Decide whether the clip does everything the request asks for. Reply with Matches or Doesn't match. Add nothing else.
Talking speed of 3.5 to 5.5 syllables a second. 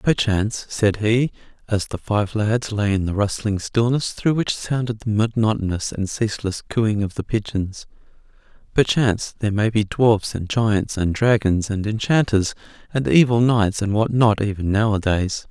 Matches